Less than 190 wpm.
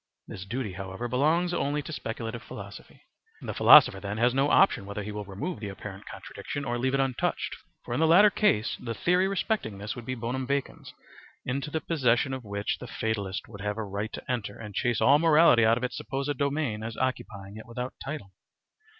No: fast, 205 wpm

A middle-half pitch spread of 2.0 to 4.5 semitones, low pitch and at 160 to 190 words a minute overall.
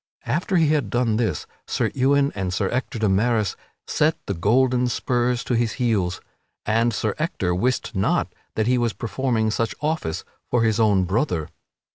Yes: average, 3.8 semitones; low, 115 Hz; average, 170 wpm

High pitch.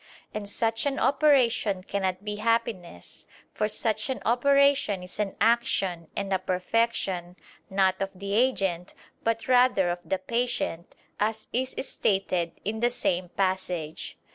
Yes: high, 205 Hz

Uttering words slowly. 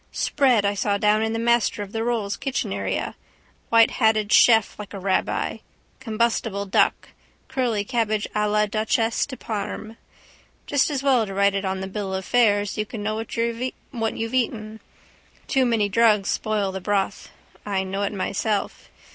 No: average, 170 wpm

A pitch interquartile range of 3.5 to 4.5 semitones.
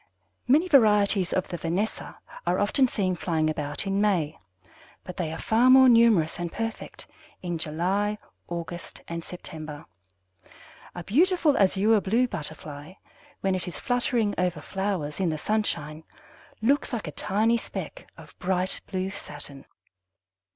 No: average, 5.2 semitones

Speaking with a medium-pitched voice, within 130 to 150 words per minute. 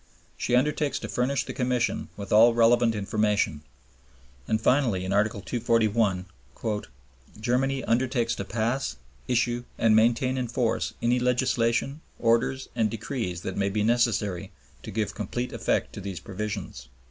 No: low, 115 Hz; average, 140 wpm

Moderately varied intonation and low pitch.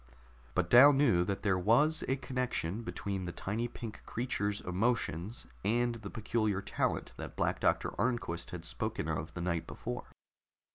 Yes: average, 4.9 semitones; low, 105 Hz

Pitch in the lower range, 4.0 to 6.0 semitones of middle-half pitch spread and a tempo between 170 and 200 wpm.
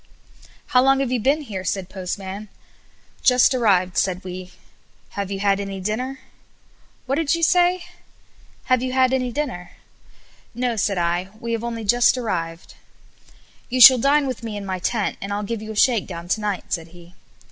No: high, 215 Hz; average, 5.2 semitones; average, 180 wpm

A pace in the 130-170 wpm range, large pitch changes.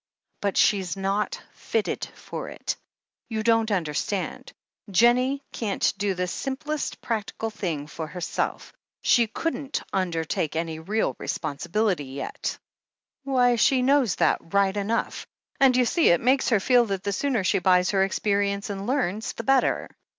No: average, 150 wpm; average, 4.9 semitones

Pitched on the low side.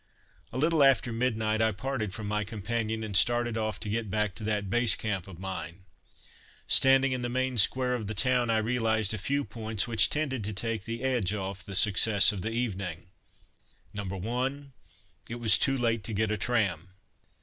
Yes: low, 110 Hz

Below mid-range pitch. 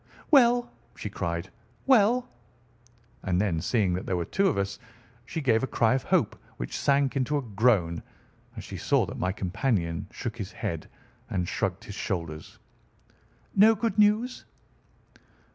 Yes: low, 115 Hz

